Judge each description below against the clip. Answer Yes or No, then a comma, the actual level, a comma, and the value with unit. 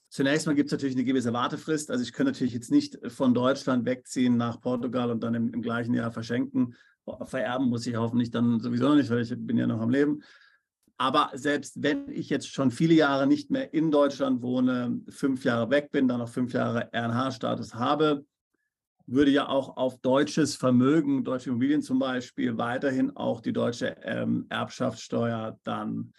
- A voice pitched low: Yes, low, 130 Hz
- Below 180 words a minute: No, average, 185 wpm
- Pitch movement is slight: No, average, 3.3 semitones